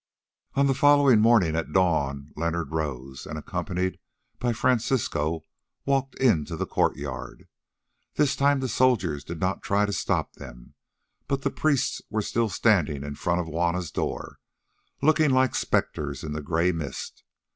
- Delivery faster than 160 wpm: No, average, 150 wpm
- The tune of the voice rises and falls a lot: Yes, wide, 9.0 semitones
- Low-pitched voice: Yes, very low, 90 Hz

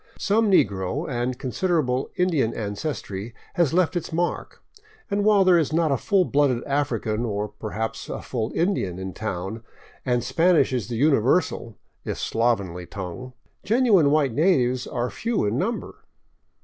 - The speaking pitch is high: No, low, 130 Hz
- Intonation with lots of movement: Yes, wide, 7.4 semitones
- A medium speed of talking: Yes, average, 150 wpm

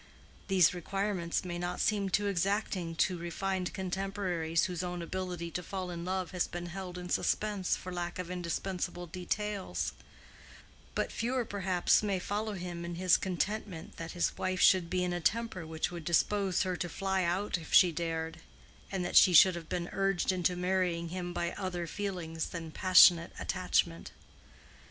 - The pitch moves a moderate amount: No, narrow, 1.9 semitones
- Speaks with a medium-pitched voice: Yes, medium, 180 Hz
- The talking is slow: No, average, 170 wpm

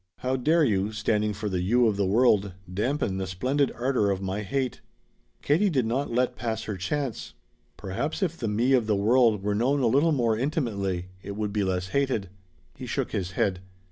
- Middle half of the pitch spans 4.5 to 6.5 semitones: Yes, average, 4.9 semitones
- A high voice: No, low, 110 Hz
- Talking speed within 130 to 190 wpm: No, average, 200 wpm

